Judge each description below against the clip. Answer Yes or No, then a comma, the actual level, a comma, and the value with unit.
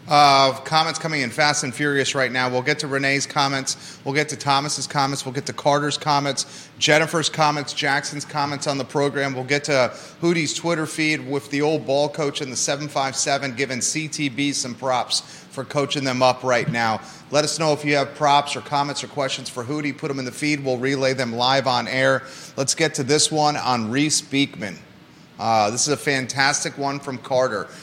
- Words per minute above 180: Yes, fast, 205 wpm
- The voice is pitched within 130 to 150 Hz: Yes, medium, 140 Hz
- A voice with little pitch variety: Yes, narrow, 1.8 semitones